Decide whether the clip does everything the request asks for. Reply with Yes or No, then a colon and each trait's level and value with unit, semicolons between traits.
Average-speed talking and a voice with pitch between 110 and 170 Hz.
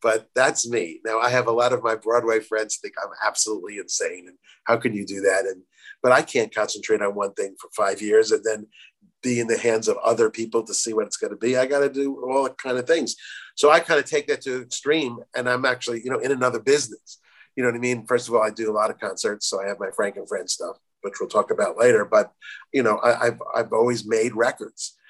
No: fast, 265 wpm; low, 135 Hz